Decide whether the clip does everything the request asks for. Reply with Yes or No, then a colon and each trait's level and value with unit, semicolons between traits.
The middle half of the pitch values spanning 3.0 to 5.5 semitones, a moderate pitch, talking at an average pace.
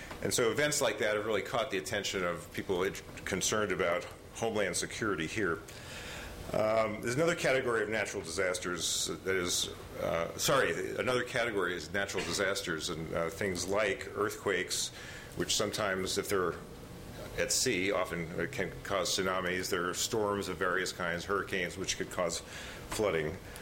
No: average, 3.9 semitones; low, 100 Hz; average, 150 wpm